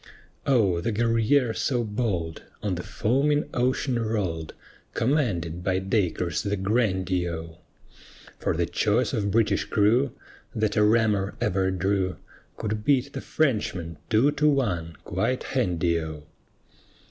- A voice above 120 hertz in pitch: No, low, 105 Hz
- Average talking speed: No, slow, 130 wpm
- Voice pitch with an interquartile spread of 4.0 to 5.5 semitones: Yes, average, 5.0 semitones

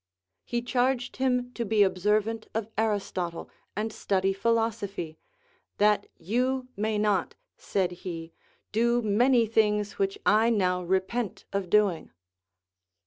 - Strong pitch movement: No, average, 3.2 semitones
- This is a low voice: No, high, 210 Hz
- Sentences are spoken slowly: Yes, slow, 120 wpm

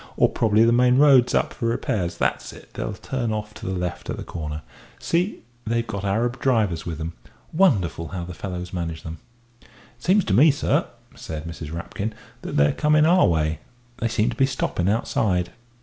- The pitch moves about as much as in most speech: No, wide, 6.3 semitones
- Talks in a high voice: No, low, 105 Hz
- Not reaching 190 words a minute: No, average, 195 wpm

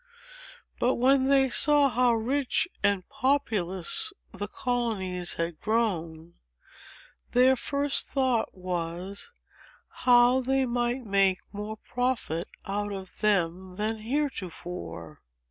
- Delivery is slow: Yes, slow, 105 wpm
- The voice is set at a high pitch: Yes, high, 220 Hz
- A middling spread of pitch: No, wide, 5.8 semitones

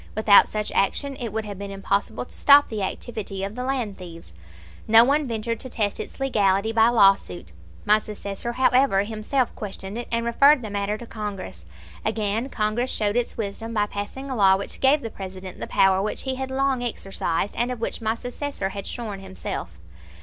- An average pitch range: Yes, average, 3.6 semitones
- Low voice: No, high, 215 Hz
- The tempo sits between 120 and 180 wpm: No, average, 195 wpm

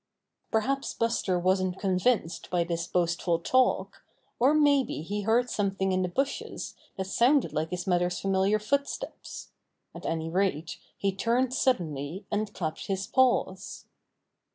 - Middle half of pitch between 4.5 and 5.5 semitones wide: Yes, average, 5.2 semitones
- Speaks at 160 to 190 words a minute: No, average, 140 wpm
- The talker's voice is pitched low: No, high, 195 Hz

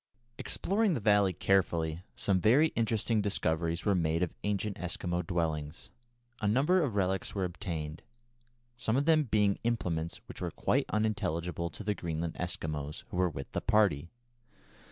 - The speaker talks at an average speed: Yes, average, 155 wpm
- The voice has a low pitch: Yes, very low, 95 Hz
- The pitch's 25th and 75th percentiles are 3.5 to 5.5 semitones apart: Yes, average, 4.4 semitones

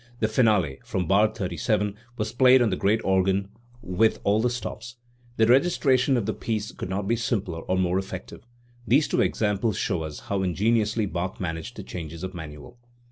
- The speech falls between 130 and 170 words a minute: No, average, 190 wpm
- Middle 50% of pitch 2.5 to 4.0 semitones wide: Yes, average, 3.6 semitones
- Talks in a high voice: No, low, 105 Hz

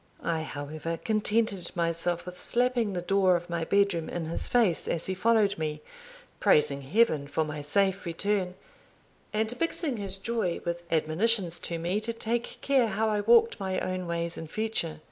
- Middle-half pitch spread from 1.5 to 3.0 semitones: No, average, 4.6 semitones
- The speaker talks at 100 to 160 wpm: No, average, 170 wpm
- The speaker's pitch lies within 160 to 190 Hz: Yes, medium, 185 Hz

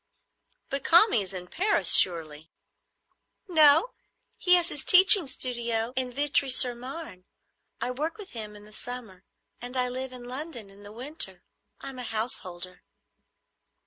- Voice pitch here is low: No, very high, 250 Hz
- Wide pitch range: Yes, wide, 5.8 semitones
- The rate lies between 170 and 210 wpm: No, average, 145 wpm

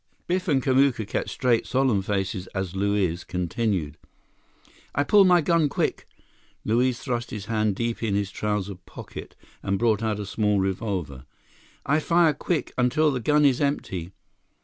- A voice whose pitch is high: No, low, 110 Hz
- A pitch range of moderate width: No, wide, 6.0 semitones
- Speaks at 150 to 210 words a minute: Yes, average, 155 wpm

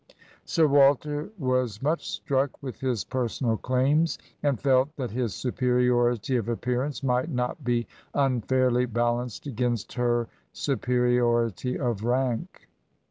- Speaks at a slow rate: Yes, slow, 130 wpm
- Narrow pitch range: Yes, narrow, 2.0 semitones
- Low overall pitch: Yes, low, 125 Hz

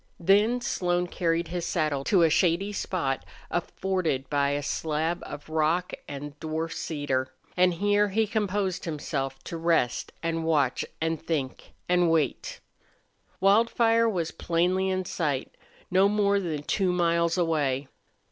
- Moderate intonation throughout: Yes, average, 3.7 semitones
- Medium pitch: Yes, medium, 170 Hz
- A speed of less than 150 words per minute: Yes, average, 140 wpm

